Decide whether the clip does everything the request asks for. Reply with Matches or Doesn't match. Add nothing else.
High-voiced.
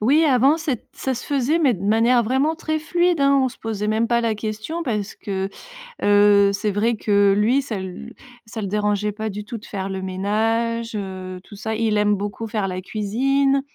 Matches